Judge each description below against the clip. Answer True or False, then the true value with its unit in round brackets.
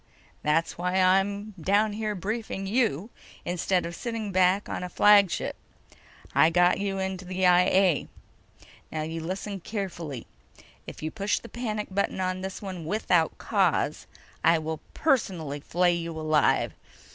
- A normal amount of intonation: True (3.2 semitones)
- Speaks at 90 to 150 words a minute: True (145 wpm)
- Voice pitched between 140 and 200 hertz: True (185 Hz)